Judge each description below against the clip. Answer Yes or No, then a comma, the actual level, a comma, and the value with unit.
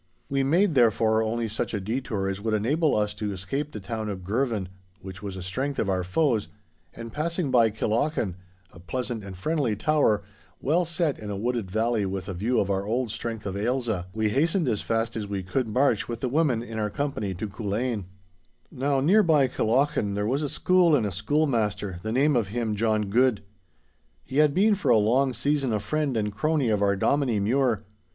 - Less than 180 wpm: No, fast, 205 wpm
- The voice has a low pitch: Yes, low, 115 Hz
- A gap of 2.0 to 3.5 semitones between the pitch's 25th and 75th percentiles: No, average, 5.0 semitones